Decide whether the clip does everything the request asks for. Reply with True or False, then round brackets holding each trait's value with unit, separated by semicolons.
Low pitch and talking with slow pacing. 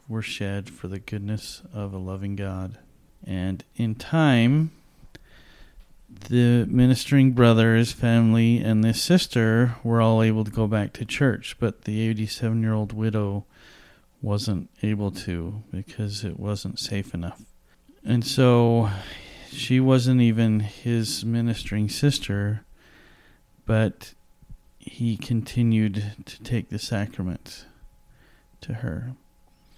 True (110 Hz; 115 wpm)